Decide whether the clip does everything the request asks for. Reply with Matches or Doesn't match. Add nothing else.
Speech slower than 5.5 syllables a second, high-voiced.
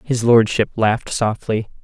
Doesn't match